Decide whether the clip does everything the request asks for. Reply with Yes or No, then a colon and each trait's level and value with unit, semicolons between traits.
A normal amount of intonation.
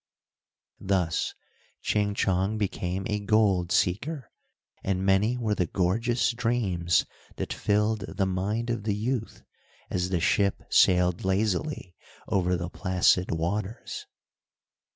Yes: average, 3.2 semitones